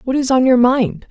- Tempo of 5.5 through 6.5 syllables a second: No, 5.0 syllables/s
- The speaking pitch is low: No, very high, 250 Hz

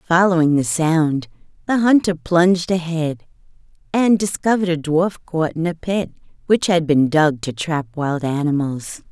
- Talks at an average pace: Yes, average, 150 wpm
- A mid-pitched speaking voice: Yes, medium, 165 Hz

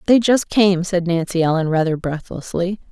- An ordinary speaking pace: Yes, average, 165 wpm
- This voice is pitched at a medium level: Yes, medium, 180 Hz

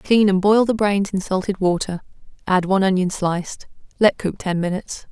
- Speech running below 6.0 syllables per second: Yes, 5.3 syllables/s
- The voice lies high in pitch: Yes, high, 195 Hz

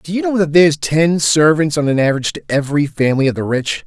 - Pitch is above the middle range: No, medium, 155 Hz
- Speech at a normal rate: No, fast, 250 wpm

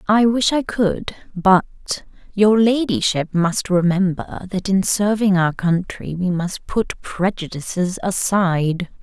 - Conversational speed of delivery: No, slow, 125 wpm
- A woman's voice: Yes, female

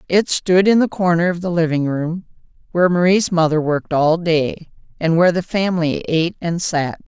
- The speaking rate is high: No, average, 185 wpm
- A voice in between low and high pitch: Yes, medium, 170 Hz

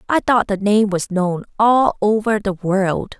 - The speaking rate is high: No, average, 190 wpm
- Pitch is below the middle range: No, high, 205 Hz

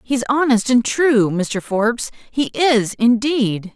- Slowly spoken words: Yes, slow, 130 wpm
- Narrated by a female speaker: Yes, female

